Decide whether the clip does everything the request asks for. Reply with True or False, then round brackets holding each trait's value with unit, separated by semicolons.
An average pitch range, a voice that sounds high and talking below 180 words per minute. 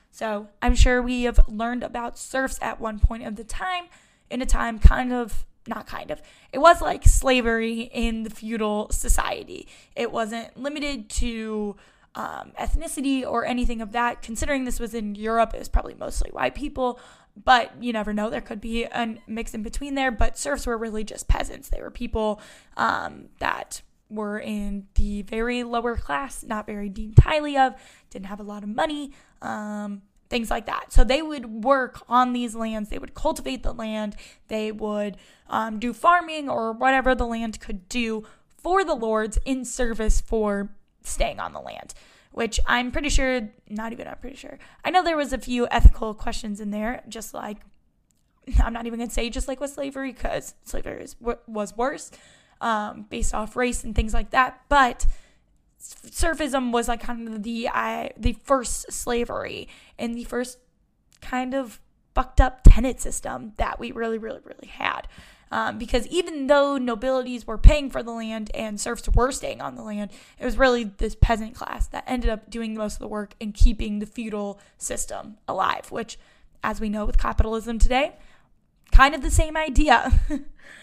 False (3.1 semitones; 235 Hz; 185 wpm)